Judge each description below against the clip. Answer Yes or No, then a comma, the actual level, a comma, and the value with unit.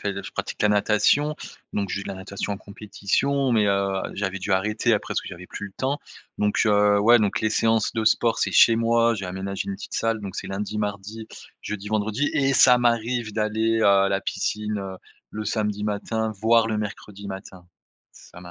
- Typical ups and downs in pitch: No, narrow, 2.3 semitones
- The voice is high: No, low, 105 Hz